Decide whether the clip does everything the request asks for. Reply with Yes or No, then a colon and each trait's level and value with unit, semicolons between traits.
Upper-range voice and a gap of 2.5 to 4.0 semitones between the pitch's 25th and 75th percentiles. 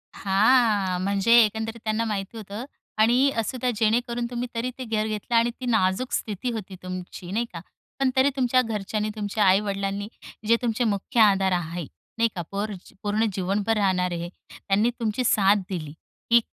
Yes: high, 215 Hz; average, 3.0 semitones